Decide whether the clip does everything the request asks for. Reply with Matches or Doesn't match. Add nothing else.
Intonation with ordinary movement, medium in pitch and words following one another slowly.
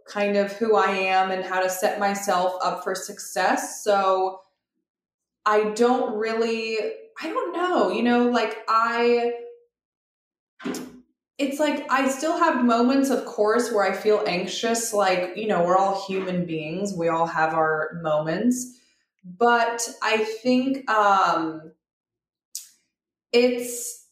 Doesn't match